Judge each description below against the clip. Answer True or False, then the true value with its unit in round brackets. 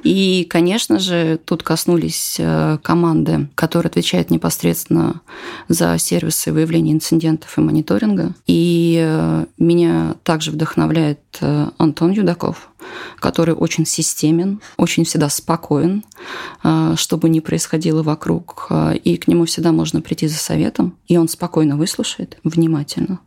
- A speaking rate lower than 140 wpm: True (115 wpm)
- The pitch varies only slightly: True (2.3 semitones)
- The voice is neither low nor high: True (160 Hz)